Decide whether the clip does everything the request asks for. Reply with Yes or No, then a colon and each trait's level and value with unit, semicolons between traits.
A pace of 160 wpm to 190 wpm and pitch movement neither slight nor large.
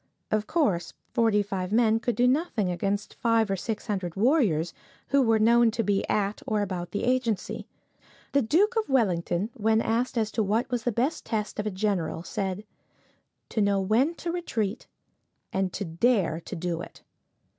Yes: average, 175 wpm; average, 3.7 semitones